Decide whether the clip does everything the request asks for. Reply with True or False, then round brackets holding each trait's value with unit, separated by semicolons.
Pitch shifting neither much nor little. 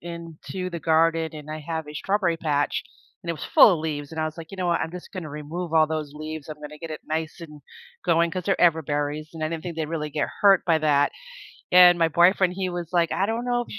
False (2.3 semitones)